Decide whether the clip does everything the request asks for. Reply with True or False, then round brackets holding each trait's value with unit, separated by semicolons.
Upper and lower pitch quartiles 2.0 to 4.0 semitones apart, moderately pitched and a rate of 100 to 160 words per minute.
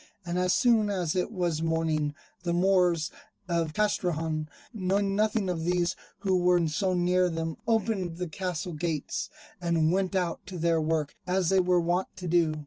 False (2.4 semitones; 175 Hz; 170 wpm)